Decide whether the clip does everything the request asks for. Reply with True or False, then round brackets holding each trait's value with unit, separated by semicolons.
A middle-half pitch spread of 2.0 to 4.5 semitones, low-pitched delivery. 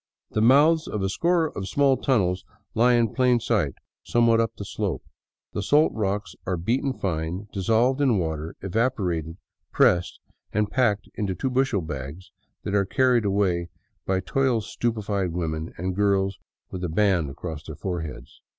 False (5.1 semitones; 100 Hz)